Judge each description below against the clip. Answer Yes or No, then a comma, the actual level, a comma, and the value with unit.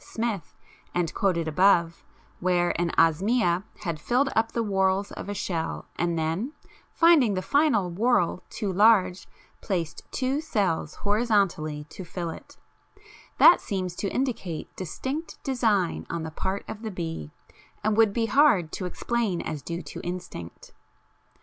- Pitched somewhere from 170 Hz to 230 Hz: Yes, high, 190 Hz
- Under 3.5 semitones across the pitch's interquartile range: No, average, 4.9 semitones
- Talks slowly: No, average, 145 wpm